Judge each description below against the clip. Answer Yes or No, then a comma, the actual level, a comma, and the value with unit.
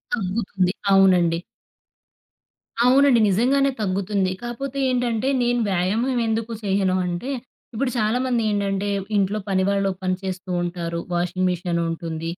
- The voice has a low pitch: No, high, 195 Hz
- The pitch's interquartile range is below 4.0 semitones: No, average, 4.3 semitones